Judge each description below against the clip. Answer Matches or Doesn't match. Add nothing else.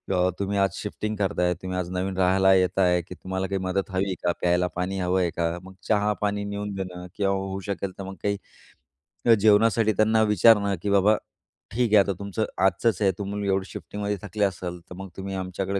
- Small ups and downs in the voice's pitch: Matches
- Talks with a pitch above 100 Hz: Doesn't match